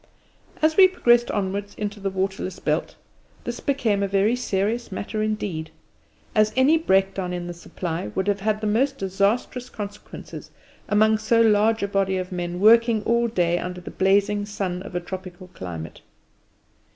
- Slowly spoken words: No, average, 165 wpm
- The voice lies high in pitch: Yes, high, 200 Hz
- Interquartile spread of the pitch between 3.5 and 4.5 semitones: No, average, 2.9 semitones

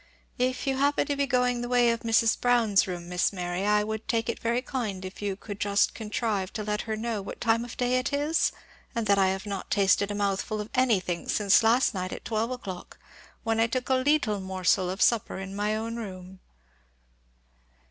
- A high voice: Yes, high, 220 Hz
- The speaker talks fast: Yes, fast, 210 wpm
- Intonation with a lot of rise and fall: No, average, 3.7 semitones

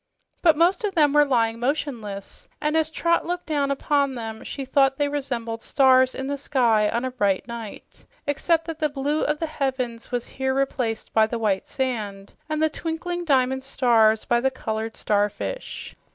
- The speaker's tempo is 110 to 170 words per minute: No, average, 180 wpm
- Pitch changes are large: No, average, 4.5 semitones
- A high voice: Yes, very high, 265 Hz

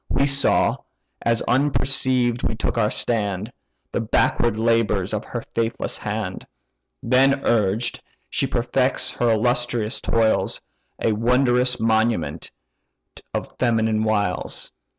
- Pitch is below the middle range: Yes, low, 115 Hz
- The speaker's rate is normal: No, slow, 110 wpm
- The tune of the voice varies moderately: No, narrow, 2.2 semitones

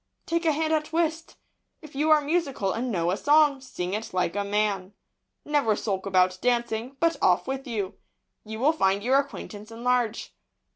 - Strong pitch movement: Yes, wide, 6.6 semitones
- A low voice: No, high, 240 Hz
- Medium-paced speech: Yes, average, 180 wpm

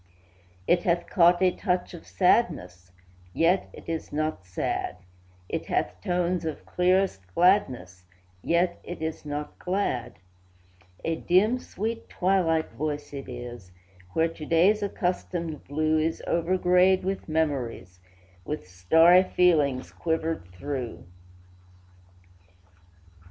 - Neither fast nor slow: No, slow, 115 wpm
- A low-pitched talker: No, medium, 165 Hz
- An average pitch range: Yes, average, 4.4 semitones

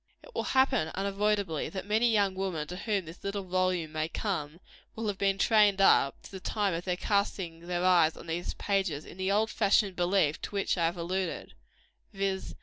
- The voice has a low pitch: No, high, 190 Hz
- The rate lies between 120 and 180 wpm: No, average, 195 wpm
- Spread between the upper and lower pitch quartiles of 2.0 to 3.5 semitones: Yes, average, 2.7 semitones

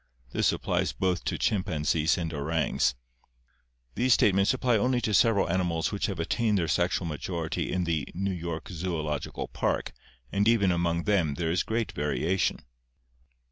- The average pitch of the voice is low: Yes, very low, 90 Hz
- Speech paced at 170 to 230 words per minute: No, average, 150 wpm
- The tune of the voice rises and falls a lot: No, average, 3.7 semitones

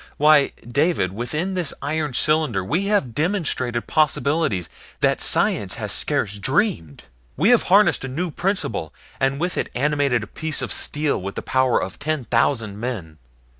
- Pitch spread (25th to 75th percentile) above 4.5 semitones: Yes, average, 5.2 semitones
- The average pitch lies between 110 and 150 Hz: Yes, medium, 140 Hz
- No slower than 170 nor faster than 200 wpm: No, average, 160 wpm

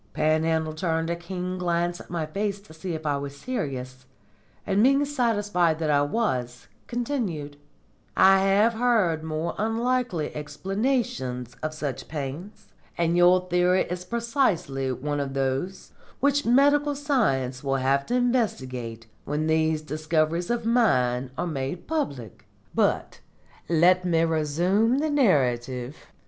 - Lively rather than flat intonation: Yes, wide, 7.0 semitones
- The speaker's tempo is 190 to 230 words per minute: No, slow, 135 wpm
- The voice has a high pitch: No, medium, 170 Hz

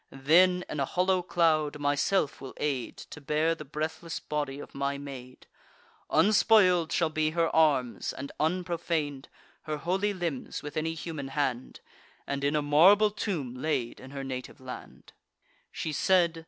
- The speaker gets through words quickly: No, average, 155 wpm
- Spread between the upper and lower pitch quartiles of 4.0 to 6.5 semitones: No, average, 3.5 semitones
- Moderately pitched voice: Yes, medium, 155 Hz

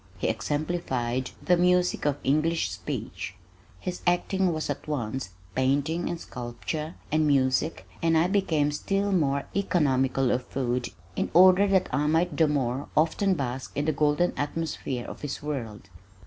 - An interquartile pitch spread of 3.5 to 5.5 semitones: Yes, average, 4.8 semitones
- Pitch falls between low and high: Yes, medium, 150 Hz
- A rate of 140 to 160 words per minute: Yes, average, 150 wpm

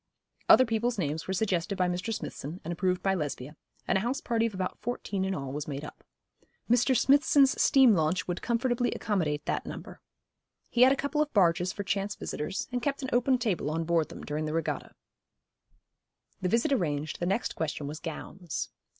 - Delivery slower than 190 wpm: No, average, 195 wpm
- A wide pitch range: Yes, wide, 6.9 semitones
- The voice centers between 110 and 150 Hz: No, high, 190 Hz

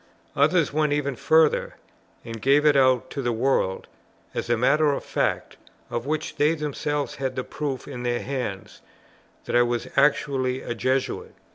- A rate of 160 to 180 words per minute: Yes, average, 165 wpm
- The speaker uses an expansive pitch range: No, average, 3.2 semitones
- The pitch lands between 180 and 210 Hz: No, low, 135 Hz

